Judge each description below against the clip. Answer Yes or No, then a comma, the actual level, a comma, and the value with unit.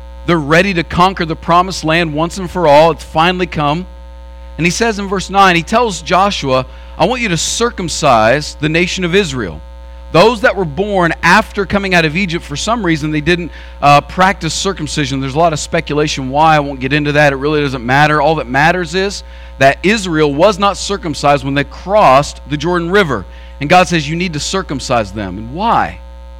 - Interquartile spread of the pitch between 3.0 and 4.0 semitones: No, average, 4.4 semitones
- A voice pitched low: No, medium, 160 Hz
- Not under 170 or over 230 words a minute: Yes, average, 200 wpm